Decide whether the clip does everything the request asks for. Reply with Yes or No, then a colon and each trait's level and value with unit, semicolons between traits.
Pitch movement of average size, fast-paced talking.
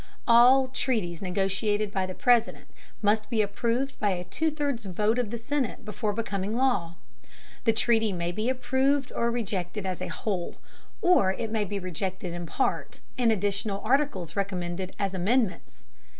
No: average, 4.2 semitones; average, 160 wpm